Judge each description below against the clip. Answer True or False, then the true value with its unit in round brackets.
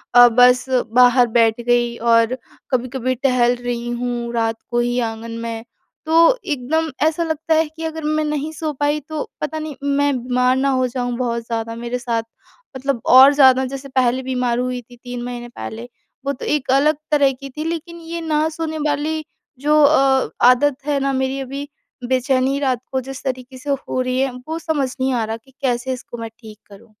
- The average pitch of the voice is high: True (260 Hz)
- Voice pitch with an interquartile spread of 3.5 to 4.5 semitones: False (3.1 semitones)